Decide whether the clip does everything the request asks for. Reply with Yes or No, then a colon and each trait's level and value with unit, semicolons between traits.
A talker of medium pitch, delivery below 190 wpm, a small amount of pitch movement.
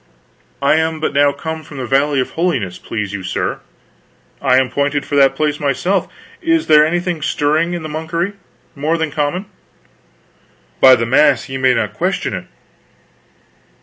No: medium, 145 Hz; average, 165 wpm; average, 3.3 semitones